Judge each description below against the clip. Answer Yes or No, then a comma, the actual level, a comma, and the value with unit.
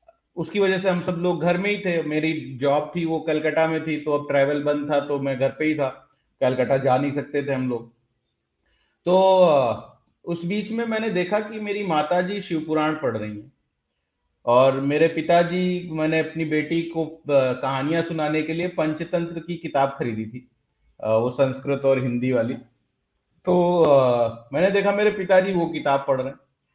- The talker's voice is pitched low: No, medium, 155 Hz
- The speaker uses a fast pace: No, average, 175 wpm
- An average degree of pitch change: Yes, average, 4.4 semitones